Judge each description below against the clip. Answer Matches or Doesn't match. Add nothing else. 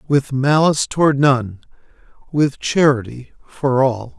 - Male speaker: Matches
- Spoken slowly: Matches